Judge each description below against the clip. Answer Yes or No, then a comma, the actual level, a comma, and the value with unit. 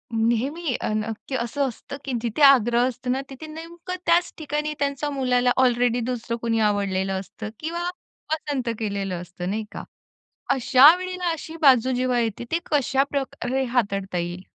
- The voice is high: Yes, very high, 250 Hz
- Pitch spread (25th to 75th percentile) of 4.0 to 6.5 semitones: Yes, average, 4.5 semitones